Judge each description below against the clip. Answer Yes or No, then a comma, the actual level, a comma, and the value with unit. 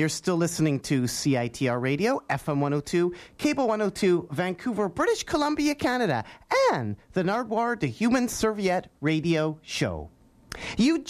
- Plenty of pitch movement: Yes, wide, 7.8 semitones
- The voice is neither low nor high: Yes, medium, 180 Hz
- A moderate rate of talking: No, slow, 125 wpm